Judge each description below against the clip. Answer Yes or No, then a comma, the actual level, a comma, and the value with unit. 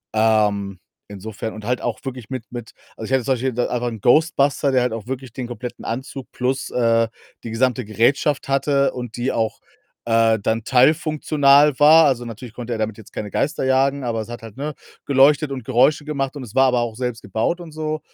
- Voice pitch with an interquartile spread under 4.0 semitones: Yes, average, 3.4 semitones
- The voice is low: Yes, low, 125 Hz